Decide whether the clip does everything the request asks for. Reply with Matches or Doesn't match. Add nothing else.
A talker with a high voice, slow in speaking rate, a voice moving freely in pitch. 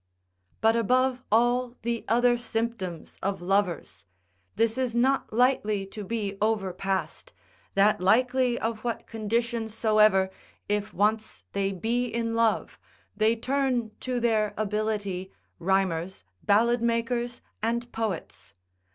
Doesn't match